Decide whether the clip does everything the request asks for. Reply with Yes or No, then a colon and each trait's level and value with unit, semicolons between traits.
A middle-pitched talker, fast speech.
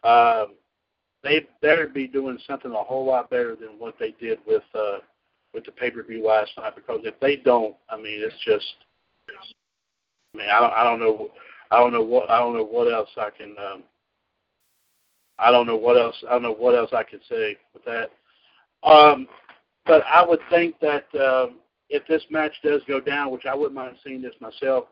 Yes: medium, 145 Hz; fast, 210 wpm